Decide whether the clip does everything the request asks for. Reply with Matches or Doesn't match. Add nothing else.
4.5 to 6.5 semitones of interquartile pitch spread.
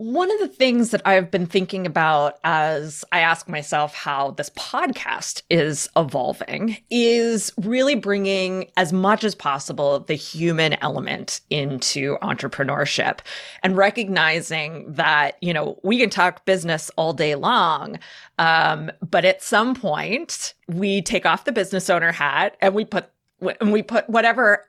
Matches